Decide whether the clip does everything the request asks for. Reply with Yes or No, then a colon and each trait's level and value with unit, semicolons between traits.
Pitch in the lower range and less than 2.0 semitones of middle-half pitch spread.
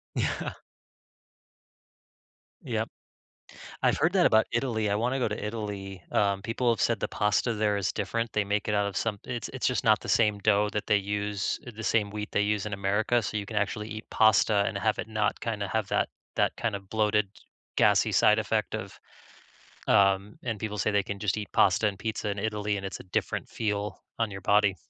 Yes: low, 105 Hz; narrow, 1.4 semitones